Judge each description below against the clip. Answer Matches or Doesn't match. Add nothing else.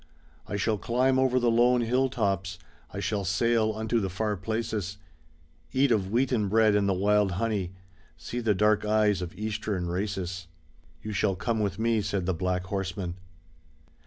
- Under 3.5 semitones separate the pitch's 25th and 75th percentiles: Matches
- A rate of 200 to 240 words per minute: Doesn't match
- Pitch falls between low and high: Doesn't match